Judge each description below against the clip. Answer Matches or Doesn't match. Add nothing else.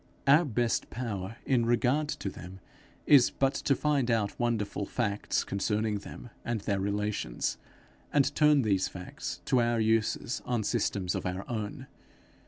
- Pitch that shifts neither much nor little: Matches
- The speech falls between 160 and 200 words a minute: Doesn't match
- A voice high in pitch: Doesn't match